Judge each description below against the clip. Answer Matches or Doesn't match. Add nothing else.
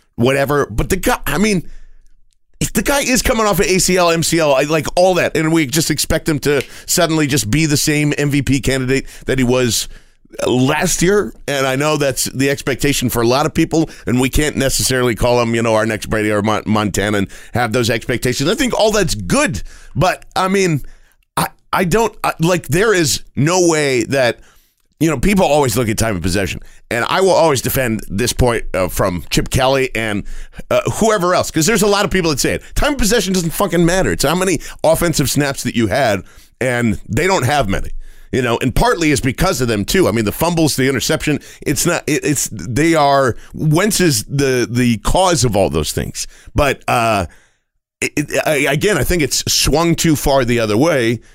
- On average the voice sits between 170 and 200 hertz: Doesn't match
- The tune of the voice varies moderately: Doesn't match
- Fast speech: Matches